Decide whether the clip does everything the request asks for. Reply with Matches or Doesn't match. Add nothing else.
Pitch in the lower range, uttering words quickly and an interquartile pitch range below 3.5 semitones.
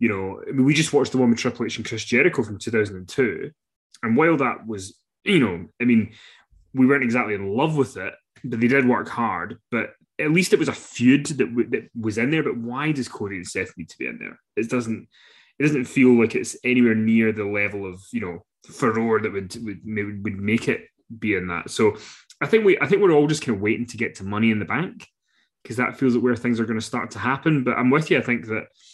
Matches